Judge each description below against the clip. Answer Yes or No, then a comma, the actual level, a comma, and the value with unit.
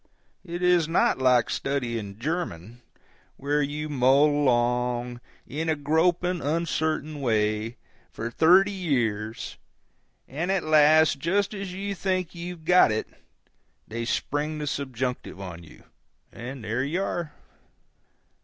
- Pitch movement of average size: No, wide, 5.8 semitones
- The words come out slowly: Yes, slow, 125 wpm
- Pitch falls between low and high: Yes, medium, 145 Hz